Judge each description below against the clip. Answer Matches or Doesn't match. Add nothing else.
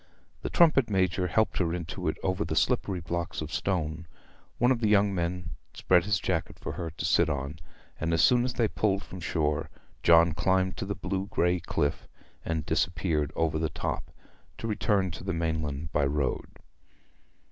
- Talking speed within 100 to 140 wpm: Doesn't match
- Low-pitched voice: Matches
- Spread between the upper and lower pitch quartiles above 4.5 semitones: Doesn't match